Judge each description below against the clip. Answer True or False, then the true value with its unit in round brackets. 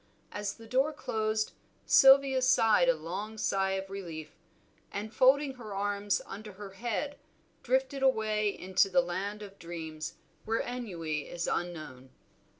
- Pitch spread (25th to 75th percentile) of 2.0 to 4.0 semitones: False (4.7 semitones)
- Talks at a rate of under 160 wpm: True (140 wpm)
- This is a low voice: False (205 Hz)